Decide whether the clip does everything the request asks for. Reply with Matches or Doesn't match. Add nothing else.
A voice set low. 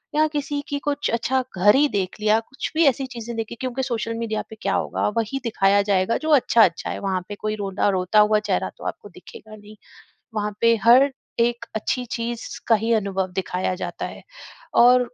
Doesn't match